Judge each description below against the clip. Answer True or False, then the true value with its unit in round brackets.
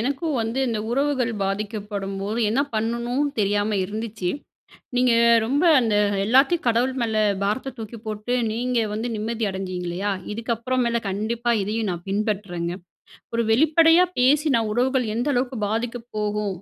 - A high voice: True (230 Hz)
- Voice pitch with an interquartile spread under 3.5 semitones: True (3.1 semitones)